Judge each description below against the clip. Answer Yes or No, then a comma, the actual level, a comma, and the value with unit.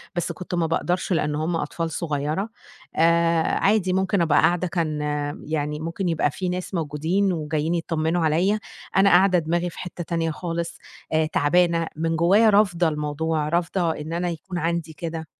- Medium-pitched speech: Yes, medium, 170 Hz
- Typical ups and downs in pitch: No, narrow, 2.0 semitones